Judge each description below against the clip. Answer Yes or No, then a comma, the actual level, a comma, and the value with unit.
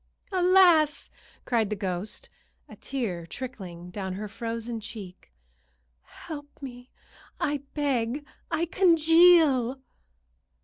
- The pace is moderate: No, slow, 95 wpm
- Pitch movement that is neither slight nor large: No, wide, 6.6 semitones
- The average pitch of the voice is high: Yes, very high, 250 Hz